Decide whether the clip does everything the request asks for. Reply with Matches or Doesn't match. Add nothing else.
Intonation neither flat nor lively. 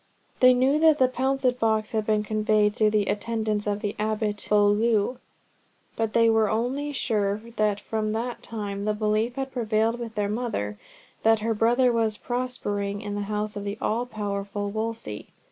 Doesn't match